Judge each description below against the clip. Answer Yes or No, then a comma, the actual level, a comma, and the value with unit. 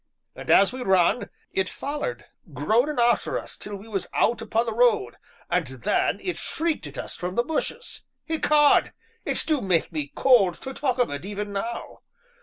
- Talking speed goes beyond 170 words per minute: Yes, average, 180 wpm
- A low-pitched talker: No, high, 235 Hz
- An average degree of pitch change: No, wide, 6.5 semitones